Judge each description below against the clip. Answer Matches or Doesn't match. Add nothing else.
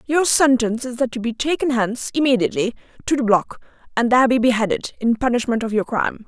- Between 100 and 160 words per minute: Doesn't match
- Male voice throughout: Doesn't match